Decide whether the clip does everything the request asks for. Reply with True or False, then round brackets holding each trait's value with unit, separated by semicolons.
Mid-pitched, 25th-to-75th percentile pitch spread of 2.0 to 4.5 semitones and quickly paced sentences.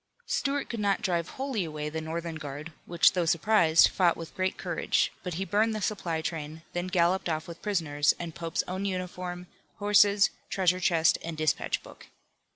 False (175 Hz; 3.1 semitones; 175 wpm)